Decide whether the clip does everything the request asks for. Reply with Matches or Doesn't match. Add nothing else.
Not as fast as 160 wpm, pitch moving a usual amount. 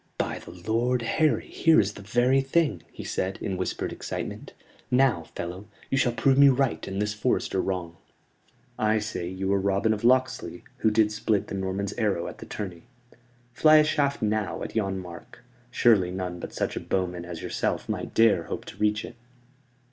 Doesn't match